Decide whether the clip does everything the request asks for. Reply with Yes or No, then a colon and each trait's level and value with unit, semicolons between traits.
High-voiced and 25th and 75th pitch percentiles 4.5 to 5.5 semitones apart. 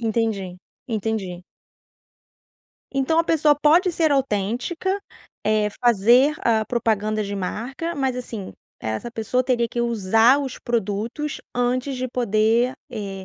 No: high, 235 Hz; average, 3.8 semitones